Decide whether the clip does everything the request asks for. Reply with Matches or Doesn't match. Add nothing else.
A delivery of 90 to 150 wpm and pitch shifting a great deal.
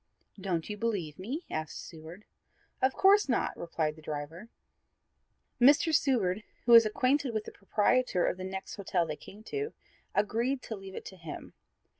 Doesn't match